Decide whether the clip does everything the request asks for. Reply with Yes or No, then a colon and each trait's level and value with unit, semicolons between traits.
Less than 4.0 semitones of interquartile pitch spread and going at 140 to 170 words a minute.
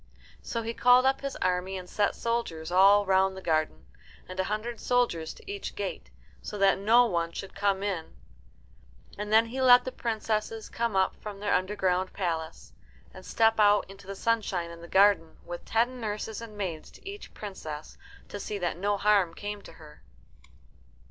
No: average, 3.5 semitones; average, 180 wpm